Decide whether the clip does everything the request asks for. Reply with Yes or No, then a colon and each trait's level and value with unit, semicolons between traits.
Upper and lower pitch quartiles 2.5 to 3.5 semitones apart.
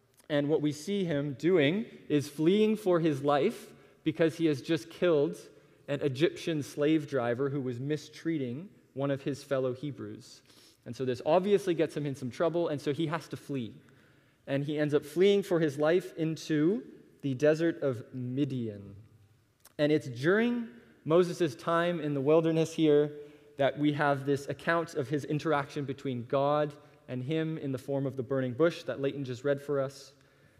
Yes: average, 2.8 semitones